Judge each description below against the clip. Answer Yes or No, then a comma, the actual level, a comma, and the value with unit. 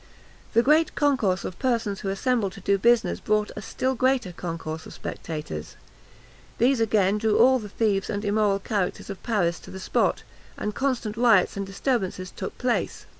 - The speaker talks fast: No, average, 175 wpm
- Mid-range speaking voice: No, high, 210 Hz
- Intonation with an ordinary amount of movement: Yes, average, 3.8 semitones